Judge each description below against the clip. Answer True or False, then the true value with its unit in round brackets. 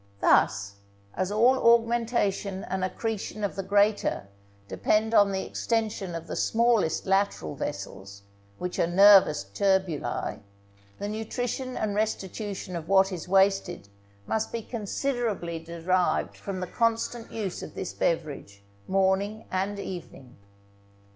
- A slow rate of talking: True (125 wpm)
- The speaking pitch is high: True (195 Hz)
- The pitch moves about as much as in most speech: True (3.8 semitones)